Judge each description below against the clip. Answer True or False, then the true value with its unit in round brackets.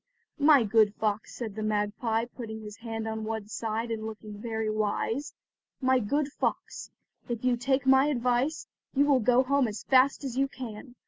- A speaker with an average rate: True (175 wpm)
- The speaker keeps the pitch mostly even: False (3.3 semitones)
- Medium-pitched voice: False (230 Hz)